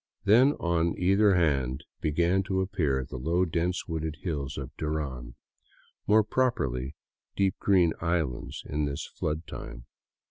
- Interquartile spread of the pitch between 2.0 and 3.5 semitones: No, average, 5.0 semitones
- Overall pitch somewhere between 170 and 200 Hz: No, very low, 80 Hz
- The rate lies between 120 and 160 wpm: Yes, slow, 135 wpm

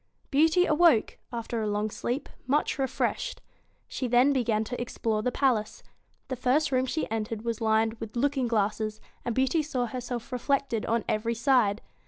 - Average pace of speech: Yes, average, 165 wpm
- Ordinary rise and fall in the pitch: Yes, average, 3.3 semitones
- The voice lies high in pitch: Yes, high, 240 Hz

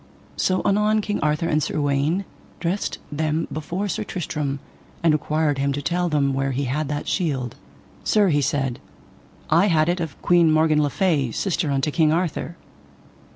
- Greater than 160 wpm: Yes, average, 170 wpm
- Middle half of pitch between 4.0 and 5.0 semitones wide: No, average, 3.4 semitones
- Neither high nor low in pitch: Yes, medium, 155 Hz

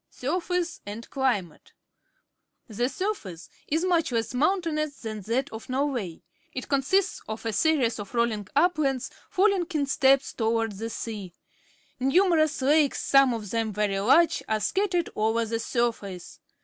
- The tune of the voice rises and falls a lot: Yes, wide, 6.0 semitones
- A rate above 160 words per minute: No, average, 140 wpm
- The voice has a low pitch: No, very high, 255 Hz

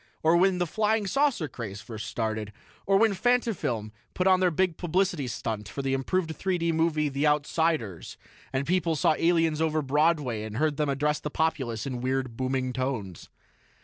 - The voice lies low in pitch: No, medium, 150 Hz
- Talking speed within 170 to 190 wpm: Yes, average, 180 wpm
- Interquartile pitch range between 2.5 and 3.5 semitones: No, average, 5.3 semitones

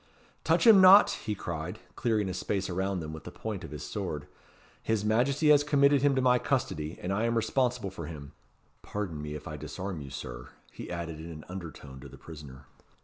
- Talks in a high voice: No, very low, 95 Hz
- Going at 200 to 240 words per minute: Yes, fast, 205 wpm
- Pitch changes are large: Yes, wide, 7.8 semitones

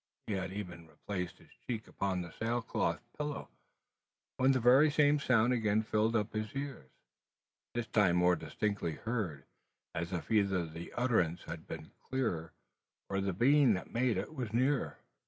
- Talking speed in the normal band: Yes, average, 165 wpm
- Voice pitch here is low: Yes, low, 105 Hz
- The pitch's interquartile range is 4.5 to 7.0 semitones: Yes, wide, 5.6 semitones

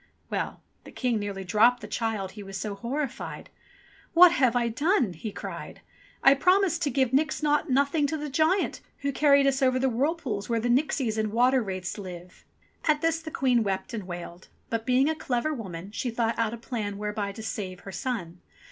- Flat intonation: No, wide, 5.4 semitones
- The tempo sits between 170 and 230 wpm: Yes, average, 200 wpm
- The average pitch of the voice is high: Yes, high, 240 Hz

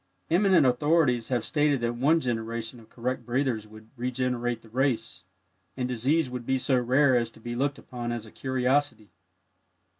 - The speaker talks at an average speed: Yes, average, 170 wpm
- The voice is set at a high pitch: No, low, 125 Hz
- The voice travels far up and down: No, narrow, 2.4 semitones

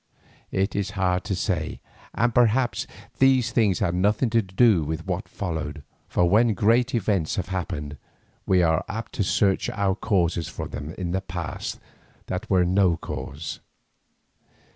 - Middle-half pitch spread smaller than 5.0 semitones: Yes, average, 3.9 semitones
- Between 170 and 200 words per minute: No, average, 155 wpm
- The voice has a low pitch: Yes, very low, 95 Hz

